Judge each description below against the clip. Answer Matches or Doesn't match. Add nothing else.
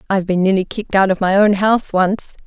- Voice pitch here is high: Matches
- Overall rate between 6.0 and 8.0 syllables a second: Matches